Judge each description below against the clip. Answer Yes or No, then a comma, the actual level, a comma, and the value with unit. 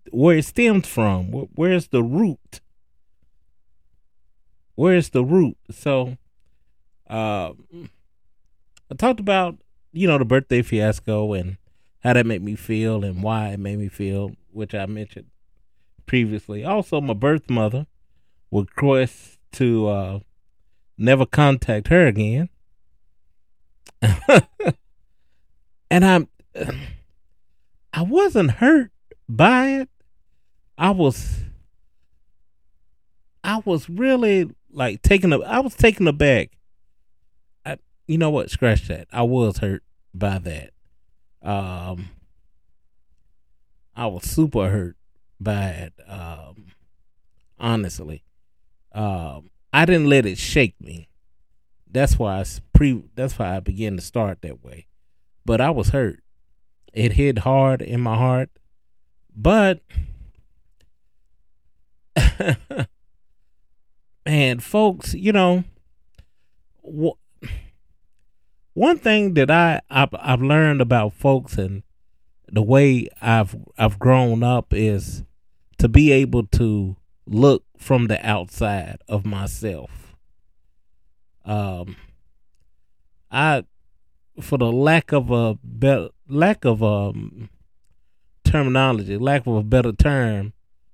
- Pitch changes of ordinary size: No, wide, 8.4 semitones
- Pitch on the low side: Yes, low, 105 Hz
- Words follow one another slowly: Yes, slow, 110 wpm